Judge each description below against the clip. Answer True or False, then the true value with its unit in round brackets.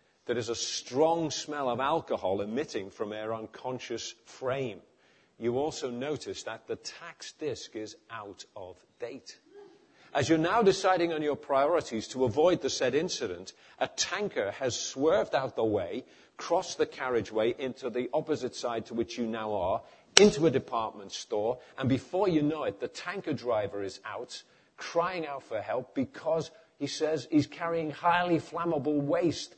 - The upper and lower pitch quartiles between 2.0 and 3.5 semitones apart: False (5.6 semitones)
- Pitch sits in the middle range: True (150 Hz)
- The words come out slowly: False (160 wpm)